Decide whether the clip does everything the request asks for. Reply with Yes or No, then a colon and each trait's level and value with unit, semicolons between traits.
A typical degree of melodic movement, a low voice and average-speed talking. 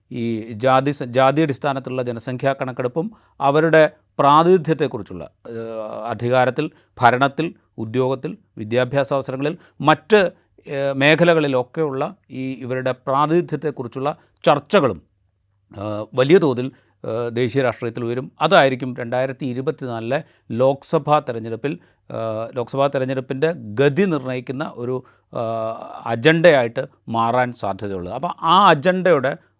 Yes: average, 4.1 semitones; low, 130 Hz; average, 85 wpm